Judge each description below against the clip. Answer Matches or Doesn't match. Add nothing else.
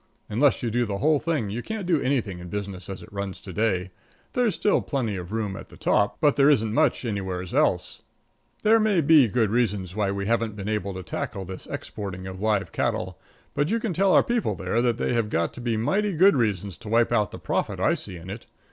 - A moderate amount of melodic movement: Doesn't match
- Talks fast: Matches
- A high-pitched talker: Doesn't match